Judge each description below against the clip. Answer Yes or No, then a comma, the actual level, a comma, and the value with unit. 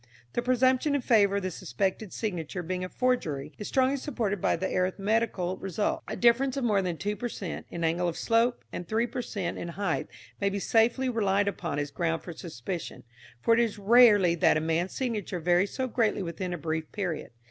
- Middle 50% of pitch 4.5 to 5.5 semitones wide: Yes, average, 4.9 semitones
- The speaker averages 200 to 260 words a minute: Yes, fast, 205 wpm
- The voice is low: No, high, 200 Hz